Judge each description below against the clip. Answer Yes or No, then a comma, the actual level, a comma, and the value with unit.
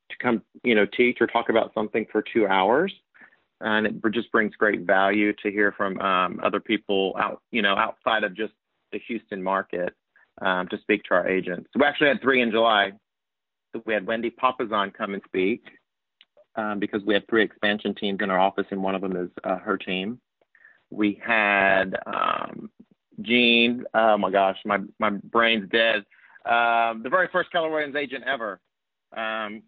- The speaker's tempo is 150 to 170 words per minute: No, average, 180 wpm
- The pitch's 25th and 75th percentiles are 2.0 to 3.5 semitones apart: Yes, average, 2.7 semitones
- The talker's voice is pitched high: No, low, 110 Hz